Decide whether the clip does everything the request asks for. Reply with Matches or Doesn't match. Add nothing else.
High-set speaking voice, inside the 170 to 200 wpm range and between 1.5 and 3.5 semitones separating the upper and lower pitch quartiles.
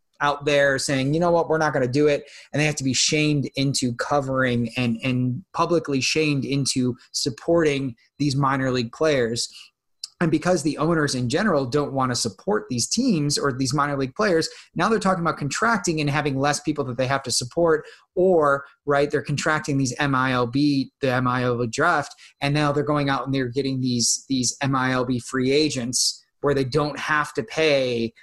Doesn't match